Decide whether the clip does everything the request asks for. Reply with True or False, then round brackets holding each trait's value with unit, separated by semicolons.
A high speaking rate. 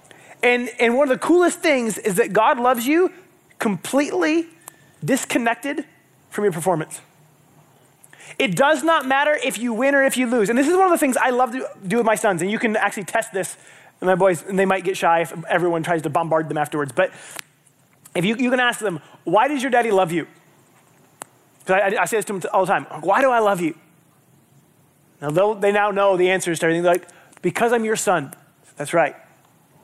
True (215 wpm)